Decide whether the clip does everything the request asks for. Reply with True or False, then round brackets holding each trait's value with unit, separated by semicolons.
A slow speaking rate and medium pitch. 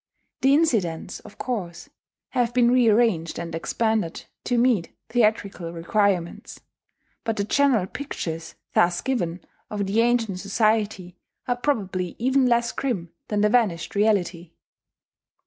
False (125 wpm; 210 Hz)